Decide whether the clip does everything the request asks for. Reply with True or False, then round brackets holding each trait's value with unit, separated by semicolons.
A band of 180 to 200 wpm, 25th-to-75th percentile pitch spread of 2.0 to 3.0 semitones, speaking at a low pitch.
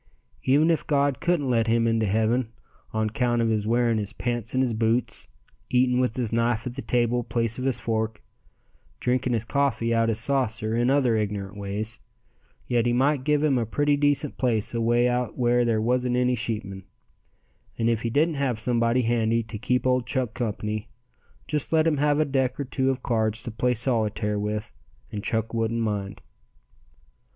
True (185 wpm; 2.5 semitones; 120 Hz)